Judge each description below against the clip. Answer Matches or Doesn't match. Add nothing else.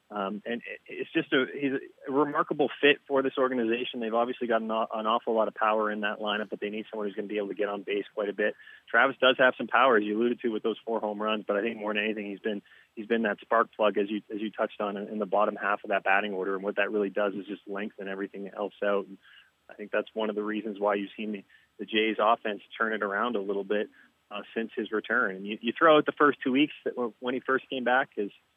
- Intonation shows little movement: Matches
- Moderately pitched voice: Doesn't match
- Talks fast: Matches